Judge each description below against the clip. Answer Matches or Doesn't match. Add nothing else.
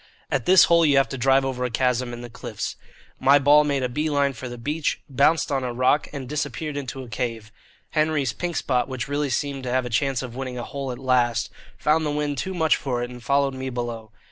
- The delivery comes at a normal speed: Doesn't match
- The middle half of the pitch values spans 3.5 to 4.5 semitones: Doesn't match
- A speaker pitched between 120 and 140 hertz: Matches